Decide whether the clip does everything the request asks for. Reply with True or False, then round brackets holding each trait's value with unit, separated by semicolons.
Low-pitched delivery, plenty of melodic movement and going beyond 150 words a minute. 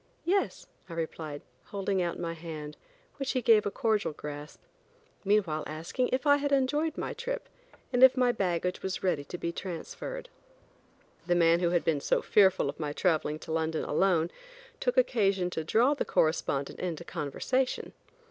False (180 Hz; 7.7 semitones; 165 wpm)